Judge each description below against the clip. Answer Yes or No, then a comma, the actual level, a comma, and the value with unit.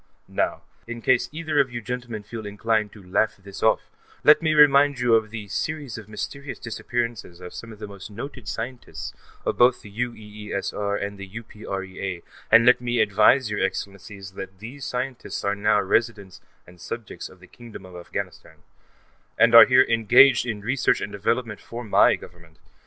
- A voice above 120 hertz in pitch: No, low, 110 Hz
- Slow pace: No, average, 180 wpm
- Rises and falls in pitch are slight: No, average, 3.4 semitones